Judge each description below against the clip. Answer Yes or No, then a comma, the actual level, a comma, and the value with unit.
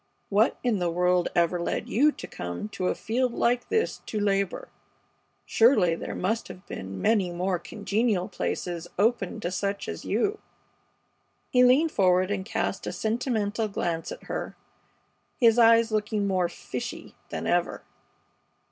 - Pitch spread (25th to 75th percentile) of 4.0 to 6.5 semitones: Yes, average, 4.3 semitones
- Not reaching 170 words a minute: Yes, average, 150 wpm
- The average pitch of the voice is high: Yes, high, 205 Hz